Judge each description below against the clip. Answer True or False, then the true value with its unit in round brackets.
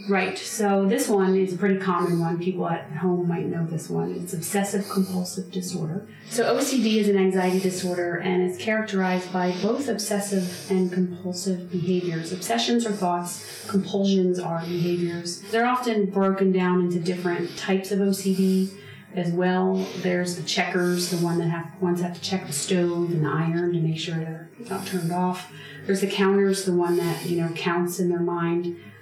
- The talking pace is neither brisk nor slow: True (180 wpm)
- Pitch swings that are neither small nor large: False (1.8 semitones)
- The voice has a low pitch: False (180 Hz)